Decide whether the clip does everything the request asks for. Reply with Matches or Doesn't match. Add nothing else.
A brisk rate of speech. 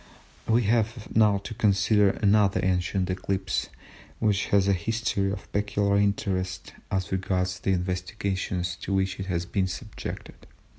Doesn't match